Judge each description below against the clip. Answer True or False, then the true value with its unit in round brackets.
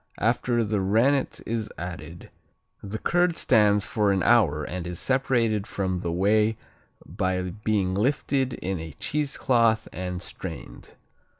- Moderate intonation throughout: True (4.2 semitones)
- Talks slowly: True (130 wpm)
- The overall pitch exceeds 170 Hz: False (105 Hz)